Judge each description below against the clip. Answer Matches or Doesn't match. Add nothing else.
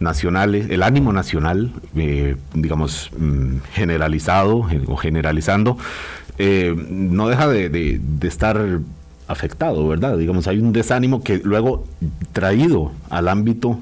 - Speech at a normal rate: Doesn't match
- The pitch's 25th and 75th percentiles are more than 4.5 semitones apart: Matches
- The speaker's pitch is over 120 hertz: Doesn't match